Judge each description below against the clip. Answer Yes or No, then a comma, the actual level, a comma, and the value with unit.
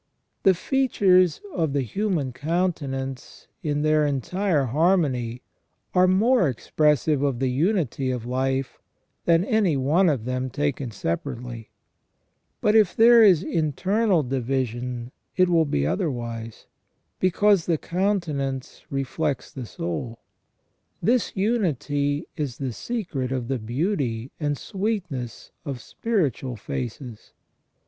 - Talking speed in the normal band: No, slow, 115 wpm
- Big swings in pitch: Yes, wide, 6.3 semitones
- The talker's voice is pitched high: No, medium, 145 Hz